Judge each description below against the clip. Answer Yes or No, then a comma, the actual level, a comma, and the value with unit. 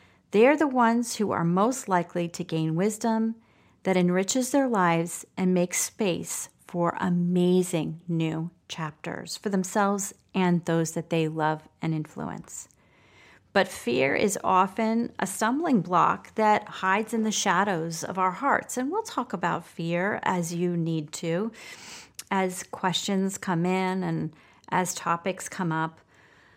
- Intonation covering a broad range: No, average, 3.9 semitones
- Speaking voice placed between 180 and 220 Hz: Yes, medium, 185 Hz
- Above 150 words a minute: No, average, 140 wpm